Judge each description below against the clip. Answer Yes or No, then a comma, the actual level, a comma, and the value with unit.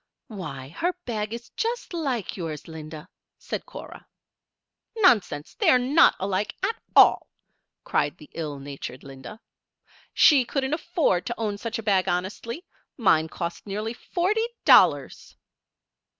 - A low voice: No, high, 210 Hz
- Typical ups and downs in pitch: No, wide, 8.6 semitones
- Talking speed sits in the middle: No, slow, 130 wpm